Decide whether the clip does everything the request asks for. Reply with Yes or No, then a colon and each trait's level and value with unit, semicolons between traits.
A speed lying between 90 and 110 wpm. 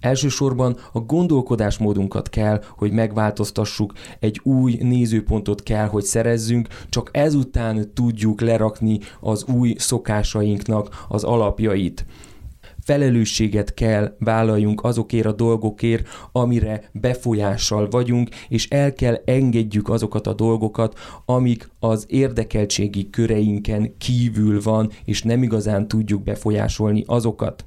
Yes: slow, 105 wpm